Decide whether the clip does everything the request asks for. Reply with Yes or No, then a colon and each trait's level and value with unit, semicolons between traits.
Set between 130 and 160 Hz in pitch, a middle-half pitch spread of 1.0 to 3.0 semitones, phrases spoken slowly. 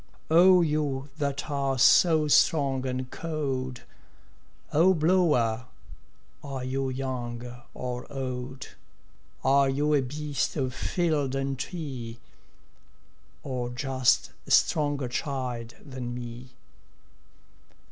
Yes: low, 135 Hz; narrow, 2.6 semitones; slow, 100 wpm